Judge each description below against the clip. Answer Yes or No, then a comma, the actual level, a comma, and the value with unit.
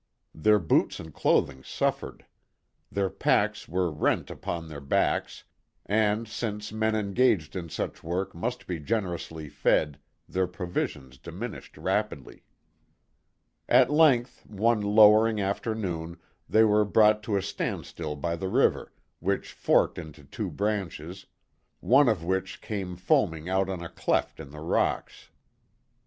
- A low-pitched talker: Yes, very low, 95 Hz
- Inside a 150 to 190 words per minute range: No, slow, 135 wpm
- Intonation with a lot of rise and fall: No, average, 4.4 semitones